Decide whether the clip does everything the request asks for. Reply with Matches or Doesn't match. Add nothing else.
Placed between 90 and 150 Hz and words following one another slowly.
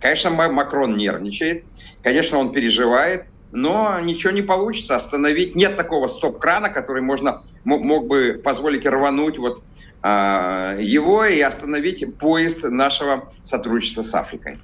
Doesn't match